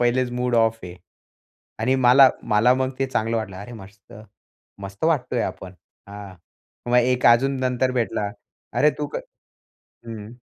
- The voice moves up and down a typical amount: Yes, average, 3.4 semitones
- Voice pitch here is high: No, low, 120 Hz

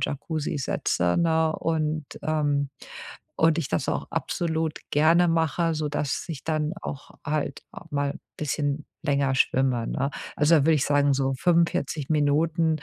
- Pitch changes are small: Yes, narrow, 2.2 semitones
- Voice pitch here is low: No, medium, 150 Hz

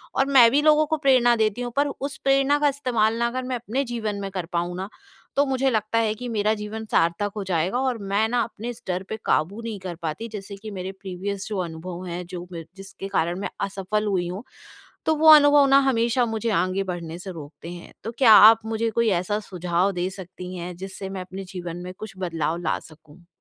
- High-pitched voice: Yes, high, 205 Hz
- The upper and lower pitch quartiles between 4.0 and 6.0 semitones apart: Yes, average, 4.7 semitones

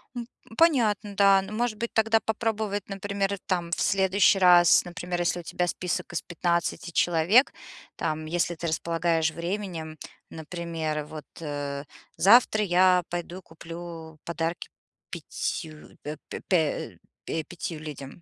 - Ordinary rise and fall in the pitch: Yes, average, 3.5 semitones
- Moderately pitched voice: Yes, medium, 175 Hz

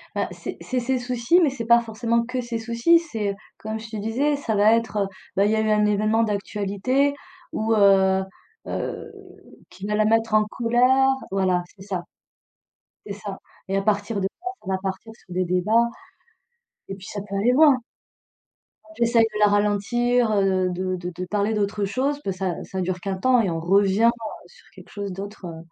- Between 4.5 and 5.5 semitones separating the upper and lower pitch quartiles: No, average, 3.2 semitones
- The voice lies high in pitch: Yes, high, 210 Hz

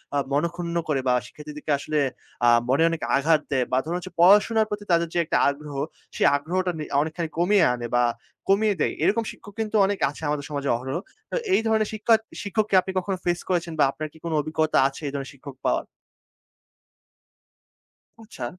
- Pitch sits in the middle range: Yes, medium, 165 Hz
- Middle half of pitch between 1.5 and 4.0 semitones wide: No, average, 5.2 semitones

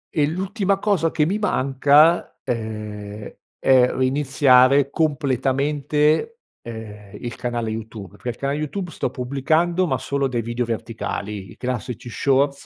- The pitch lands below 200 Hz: Yes, low, 135 Hz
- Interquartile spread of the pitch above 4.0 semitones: Yes, average, 4.4 semitones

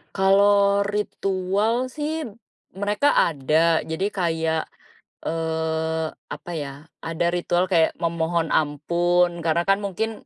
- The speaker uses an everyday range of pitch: Yes, average, 3.7 semitones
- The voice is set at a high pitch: No, medium, 175 Hz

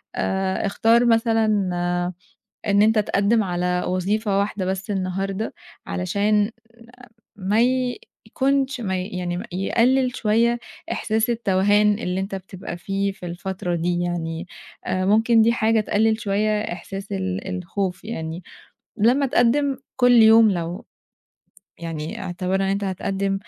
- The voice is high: Yes, high, 200 Hz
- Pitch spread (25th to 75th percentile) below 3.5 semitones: Yes, average, 3.1 semitones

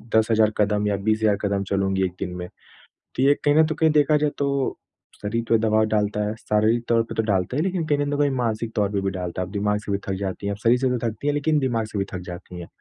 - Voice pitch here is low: Yes, low, 110 Hz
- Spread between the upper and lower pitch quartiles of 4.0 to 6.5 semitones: Yes, average, 4.7 semitones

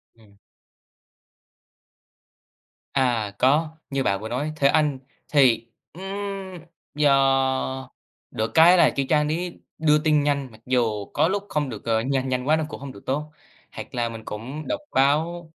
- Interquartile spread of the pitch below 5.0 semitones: Yes, average, 3.8 semitones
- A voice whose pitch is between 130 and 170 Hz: Yes, low, 135 Hz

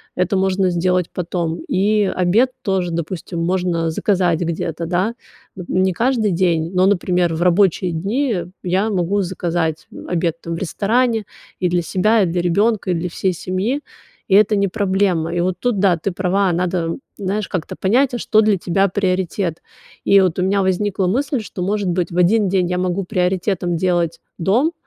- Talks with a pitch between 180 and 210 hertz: Yes, medium, 185 Hz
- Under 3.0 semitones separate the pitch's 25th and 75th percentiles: Yes, narrow, 2.6 semitones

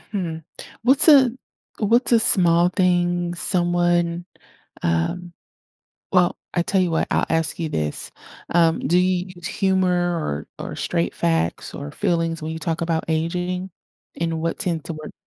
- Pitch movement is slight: Yes, narrow, 1.9 semitones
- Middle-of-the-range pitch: Yes, medium, 175 Hz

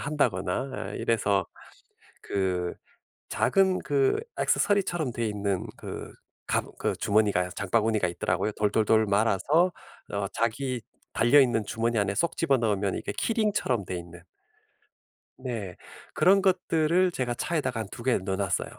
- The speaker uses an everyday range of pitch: No, wide, 6.1 semitones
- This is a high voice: No, low, 115 Hz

